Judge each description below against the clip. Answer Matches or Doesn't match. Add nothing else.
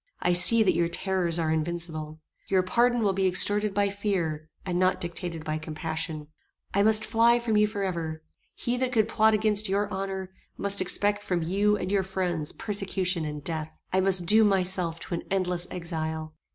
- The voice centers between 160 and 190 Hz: Matches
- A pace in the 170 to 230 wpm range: Matches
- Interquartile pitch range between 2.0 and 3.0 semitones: Doesn't match